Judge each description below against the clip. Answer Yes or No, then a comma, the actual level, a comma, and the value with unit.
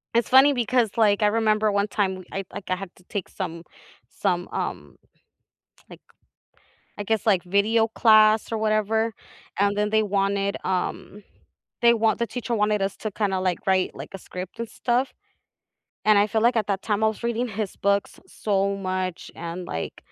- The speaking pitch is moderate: No, high, 205 Hz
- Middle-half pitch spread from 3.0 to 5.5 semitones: No, narrow, 2.4 semitones